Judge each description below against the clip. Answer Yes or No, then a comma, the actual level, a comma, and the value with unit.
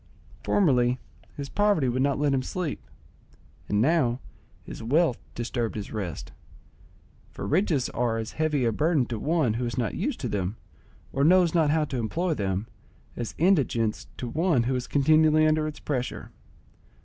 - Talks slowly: No, average, 165 wpm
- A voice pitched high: No, low, 135 Hz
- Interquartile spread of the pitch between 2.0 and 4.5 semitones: No, average, 5.0 semitones